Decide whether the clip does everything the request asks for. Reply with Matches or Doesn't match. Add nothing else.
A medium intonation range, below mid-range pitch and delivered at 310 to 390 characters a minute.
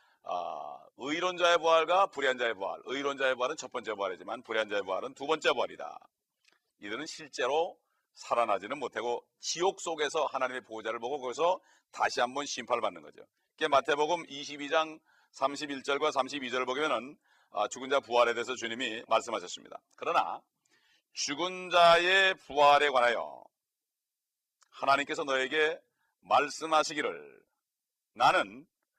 Doesn't match